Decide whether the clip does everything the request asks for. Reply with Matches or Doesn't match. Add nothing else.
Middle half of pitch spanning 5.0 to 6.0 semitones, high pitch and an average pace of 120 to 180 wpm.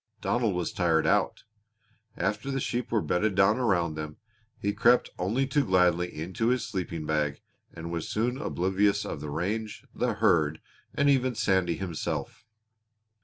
Doesn't match